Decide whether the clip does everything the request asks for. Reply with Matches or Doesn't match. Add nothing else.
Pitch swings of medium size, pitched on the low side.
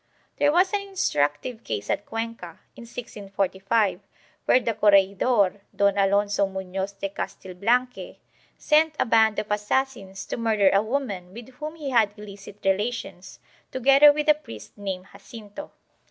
Doesn't match